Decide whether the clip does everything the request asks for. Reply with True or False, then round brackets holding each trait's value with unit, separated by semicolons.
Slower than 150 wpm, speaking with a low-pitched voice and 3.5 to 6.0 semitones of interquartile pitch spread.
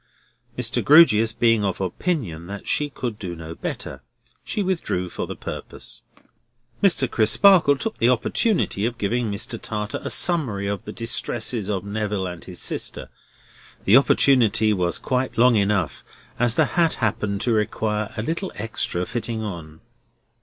False (155 wpm; 110 Hz; 4.0 semitones)